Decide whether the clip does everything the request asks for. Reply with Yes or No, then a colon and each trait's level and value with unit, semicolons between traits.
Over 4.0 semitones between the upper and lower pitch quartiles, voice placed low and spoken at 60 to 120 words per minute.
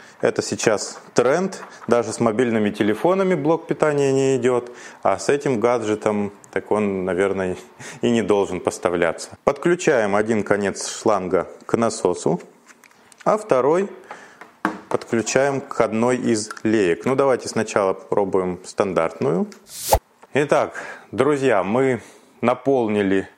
Yes: average, 4.6 semitones; low, 115 Hz; average, 115 wpm